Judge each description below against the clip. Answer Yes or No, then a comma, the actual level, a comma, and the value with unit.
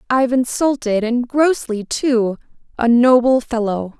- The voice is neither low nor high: No, high, 240 Hz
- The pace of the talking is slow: Yes, slow, 90 wpm